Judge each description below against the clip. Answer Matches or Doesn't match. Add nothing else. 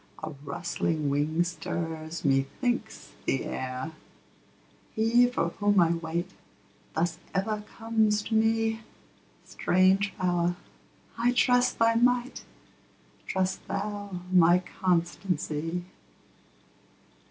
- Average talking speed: Doesn't match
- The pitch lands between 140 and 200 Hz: Matches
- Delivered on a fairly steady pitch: Doesn't match